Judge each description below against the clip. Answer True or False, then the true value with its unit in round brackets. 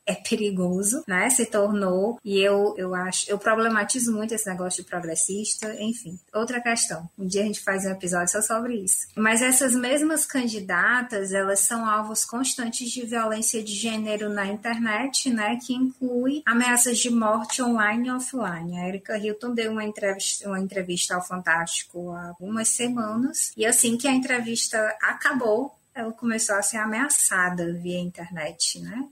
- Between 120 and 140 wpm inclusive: False (165 wpm)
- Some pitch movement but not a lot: True (3.6 semitones)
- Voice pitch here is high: True (215 Hz)